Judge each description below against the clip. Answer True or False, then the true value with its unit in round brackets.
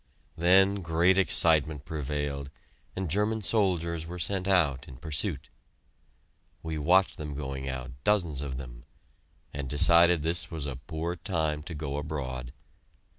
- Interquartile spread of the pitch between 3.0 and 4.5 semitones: True (3.8 semitones)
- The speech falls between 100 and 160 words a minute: True (135 wpm)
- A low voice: True (80 Hz)